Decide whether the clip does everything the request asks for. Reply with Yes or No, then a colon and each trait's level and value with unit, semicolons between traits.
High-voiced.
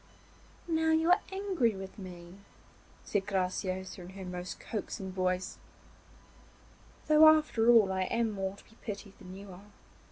Yes: high, 195 Hz